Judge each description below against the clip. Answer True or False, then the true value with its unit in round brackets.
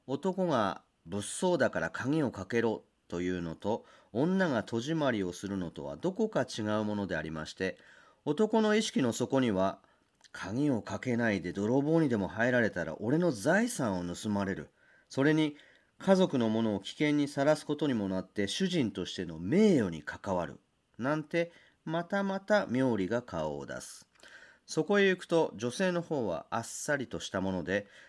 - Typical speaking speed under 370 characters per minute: True (310 characters per minute)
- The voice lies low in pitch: True (125 Hz)